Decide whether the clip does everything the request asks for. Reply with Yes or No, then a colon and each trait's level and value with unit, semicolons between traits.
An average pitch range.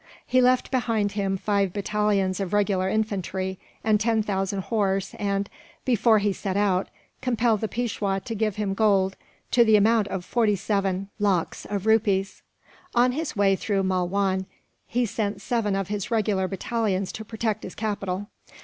No: narrow, 2.2 semitones